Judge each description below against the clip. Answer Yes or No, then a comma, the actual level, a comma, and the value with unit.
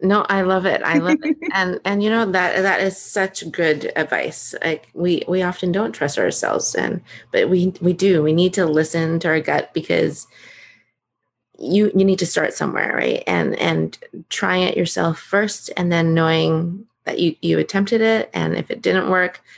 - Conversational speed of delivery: Yes, average, 195 wpm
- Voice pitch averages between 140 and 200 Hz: Yes, medium, 185 Hz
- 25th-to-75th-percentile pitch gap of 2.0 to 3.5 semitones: Yes, average, 2.8 semitones